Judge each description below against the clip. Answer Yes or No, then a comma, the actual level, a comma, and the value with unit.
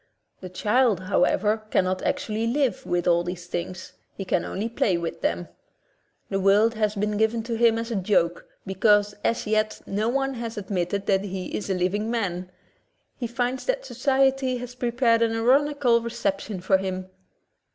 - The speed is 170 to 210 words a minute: Yes, average, 175 wpm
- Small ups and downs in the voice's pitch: No, average, 3.9 semitones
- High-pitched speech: Yes, high, 215 Hz